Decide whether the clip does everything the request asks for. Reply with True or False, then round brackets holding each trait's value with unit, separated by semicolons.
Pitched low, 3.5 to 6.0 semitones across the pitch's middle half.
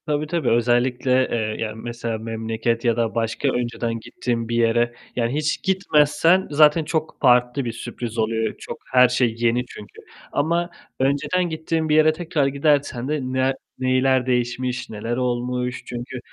True (125 Hz; 4.0 semitones)